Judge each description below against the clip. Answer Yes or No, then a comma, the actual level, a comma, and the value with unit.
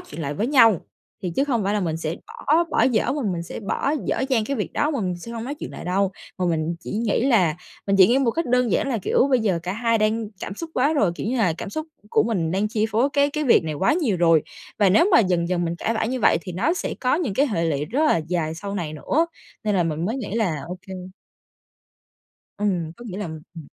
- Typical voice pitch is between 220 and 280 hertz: No, high, 205 Hz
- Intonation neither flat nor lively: No, wide, 6.4 semitones